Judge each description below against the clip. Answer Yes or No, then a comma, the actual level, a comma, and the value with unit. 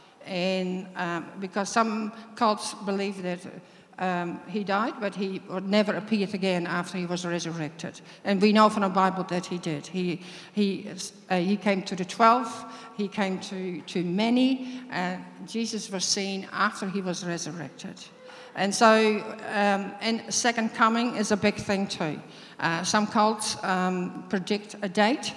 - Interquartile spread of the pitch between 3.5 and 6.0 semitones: No, average, 2.8 semitones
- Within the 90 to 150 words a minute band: No, average, 160 wpm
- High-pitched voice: Yes, high, 195 Hz